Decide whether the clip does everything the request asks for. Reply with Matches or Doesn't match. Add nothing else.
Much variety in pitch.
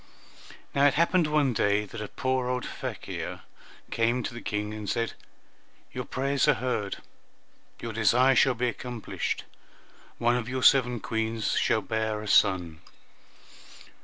Doesn't match